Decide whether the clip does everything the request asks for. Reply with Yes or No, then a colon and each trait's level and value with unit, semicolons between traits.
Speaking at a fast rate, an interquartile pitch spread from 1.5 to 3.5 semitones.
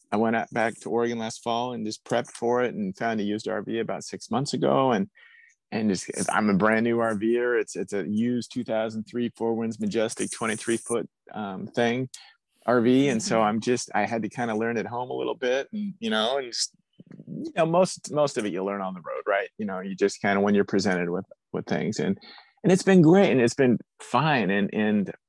Yes: fast, 235 wpm; narrow, 2.6 semitones